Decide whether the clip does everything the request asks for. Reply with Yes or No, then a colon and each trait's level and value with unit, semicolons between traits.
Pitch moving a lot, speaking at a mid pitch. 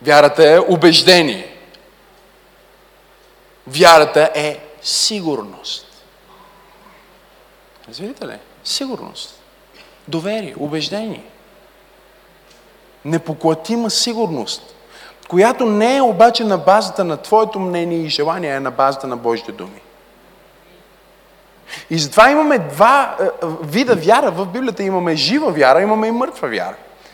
Yes: wide, 5.7 semitones; medium, 180 Hz